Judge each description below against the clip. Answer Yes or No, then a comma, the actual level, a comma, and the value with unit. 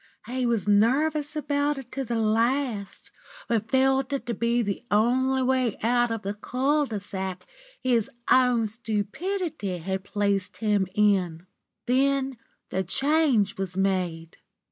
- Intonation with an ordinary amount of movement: Yes, average, 4.8 semitones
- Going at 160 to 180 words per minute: No, average, 140 wpm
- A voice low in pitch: No, high, 230 Hz